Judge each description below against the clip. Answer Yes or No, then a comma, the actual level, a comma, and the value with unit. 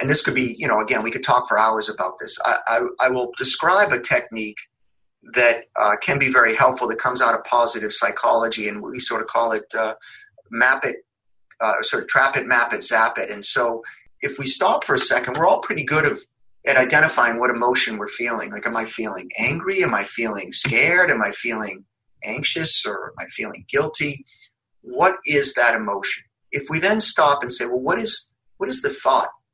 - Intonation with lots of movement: Yes, wide, 8.7 semitones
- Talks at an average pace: No, fast, 215 wpm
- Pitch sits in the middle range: No, low, 130 Hz